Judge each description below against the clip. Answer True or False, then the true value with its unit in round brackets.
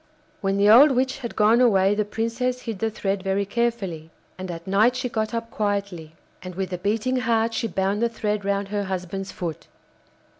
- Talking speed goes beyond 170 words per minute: True (195 wpm)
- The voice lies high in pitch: True (205 Hz)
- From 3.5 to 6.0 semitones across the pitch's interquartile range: False (3.1 semitones)